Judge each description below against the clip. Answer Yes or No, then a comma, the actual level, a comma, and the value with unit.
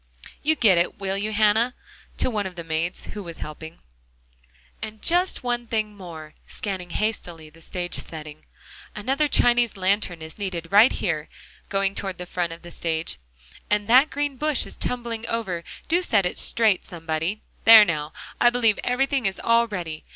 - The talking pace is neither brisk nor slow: Yes, average, 175 wpm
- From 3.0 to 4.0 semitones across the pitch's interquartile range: No, average, 5.3 semitones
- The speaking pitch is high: Yes, high, 200 Hz